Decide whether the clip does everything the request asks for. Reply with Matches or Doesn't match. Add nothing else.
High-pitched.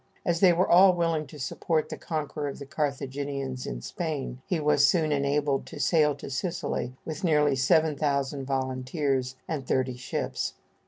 Doesn't match